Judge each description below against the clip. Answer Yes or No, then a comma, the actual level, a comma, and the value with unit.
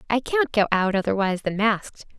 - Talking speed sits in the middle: Yes, average, 190 wpm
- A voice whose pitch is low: No, high, 215 Hz